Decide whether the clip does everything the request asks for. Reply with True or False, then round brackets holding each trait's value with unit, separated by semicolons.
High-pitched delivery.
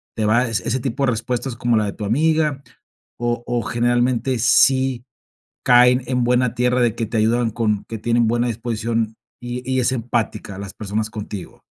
False (120 Hz)